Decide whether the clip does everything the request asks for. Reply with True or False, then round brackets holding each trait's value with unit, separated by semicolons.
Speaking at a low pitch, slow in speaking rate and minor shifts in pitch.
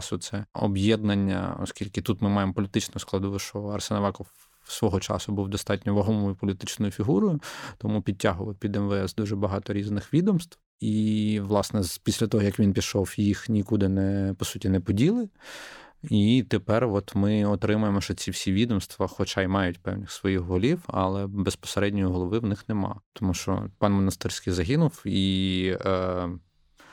False (100 Hz; 145 wpm; 1.8 semitones)